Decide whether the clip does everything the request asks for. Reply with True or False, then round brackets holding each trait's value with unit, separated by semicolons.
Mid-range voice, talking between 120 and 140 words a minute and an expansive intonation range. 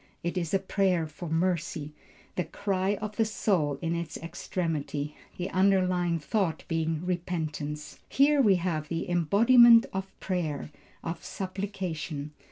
False (175 Hz; 135 wpm; 3.3 semitones)